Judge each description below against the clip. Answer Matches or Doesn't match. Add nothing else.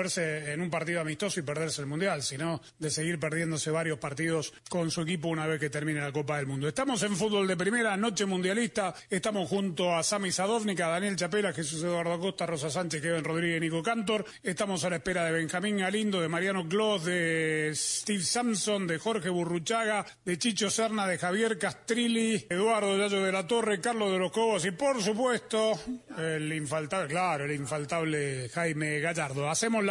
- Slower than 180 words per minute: Doesn't match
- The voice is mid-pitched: Matches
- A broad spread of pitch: Doesn't match